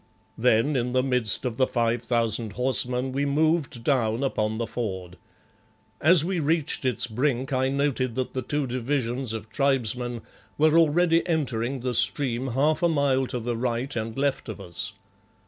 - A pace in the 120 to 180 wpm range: Yes, average, 165 wpm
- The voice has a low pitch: Yes, low, 130 Hz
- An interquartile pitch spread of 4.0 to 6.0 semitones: No, average, 3.3 semitones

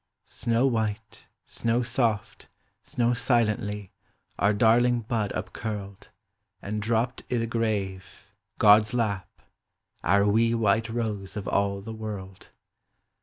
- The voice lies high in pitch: No, low, 110 Hz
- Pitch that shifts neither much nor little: No, narrow, 2.3 semitones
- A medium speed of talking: No, slow, 125 wpm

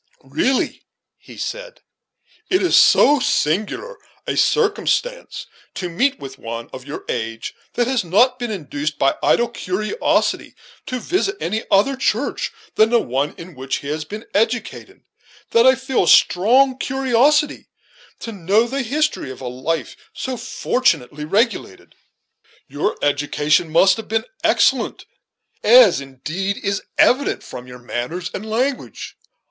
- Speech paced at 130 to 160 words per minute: Yes, average, 140 wpm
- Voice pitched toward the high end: Yes, high, 215 Hz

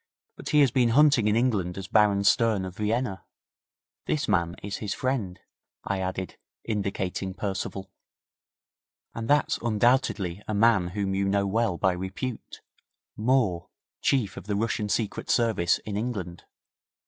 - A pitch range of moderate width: Yes, average, 3.5 semitones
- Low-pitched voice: Yes, low, 105 Hz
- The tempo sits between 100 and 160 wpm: Yes, average, 145 wpm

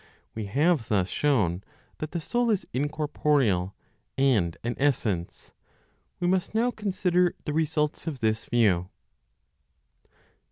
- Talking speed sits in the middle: No, slow, 120 wpm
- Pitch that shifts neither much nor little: No, wide, 8.0 semitones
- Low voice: No, medium, 145 Hz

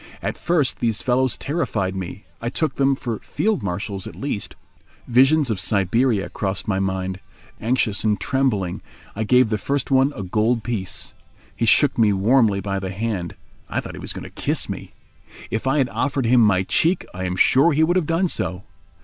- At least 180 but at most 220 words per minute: Yes, average, 190 wpm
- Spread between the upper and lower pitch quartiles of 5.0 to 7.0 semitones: Yes, wide, 5.6 semitones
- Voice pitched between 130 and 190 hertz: No, low, 115 Hz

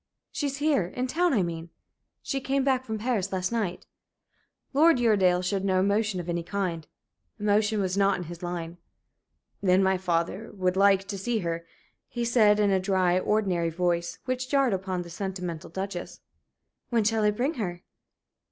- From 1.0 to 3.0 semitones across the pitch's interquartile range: No, average, 3.9 semitones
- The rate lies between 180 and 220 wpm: No, average, 170 wpm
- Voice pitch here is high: Yes, high, 195 Hz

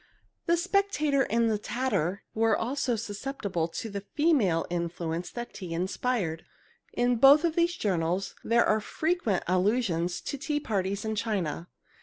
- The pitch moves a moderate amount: No, wide, 6.9 semitones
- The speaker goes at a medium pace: Yes, average, 145 wpm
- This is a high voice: Yes, high, 220 Hz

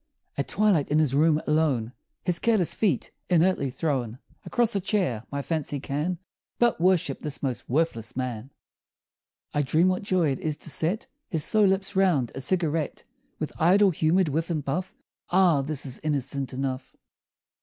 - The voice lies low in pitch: No, medium, 155 Hz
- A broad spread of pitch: No, average, 5.0 semitones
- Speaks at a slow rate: No, average, 165 wpm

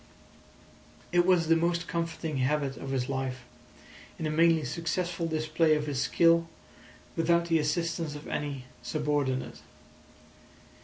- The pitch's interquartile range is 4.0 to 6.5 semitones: No, narrow, 2.5 semitones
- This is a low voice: No, medium, 155 Hz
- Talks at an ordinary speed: No, slow, 125 wpm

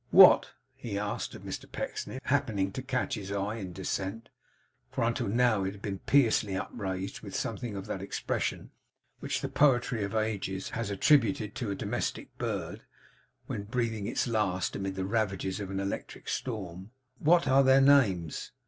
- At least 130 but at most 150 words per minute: No, average, 170 wpm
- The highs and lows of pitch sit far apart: No, average, 3.8 semitones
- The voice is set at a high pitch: No, low, 105 Hz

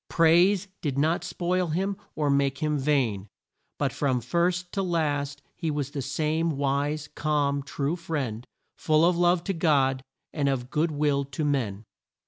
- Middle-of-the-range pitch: Yes, medium, 150 Hz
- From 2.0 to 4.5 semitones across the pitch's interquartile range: Yes, average, 3.2 semitones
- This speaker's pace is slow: No, average, 160 wpm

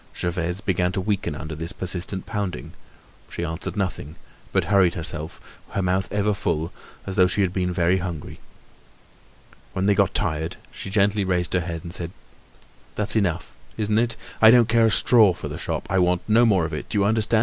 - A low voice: Yes, very low, 95 Hz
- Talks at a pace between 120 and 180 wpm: No, average, 195 wpm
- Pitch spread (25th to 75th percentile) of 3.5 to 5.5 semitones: No, average, 3.1 semitones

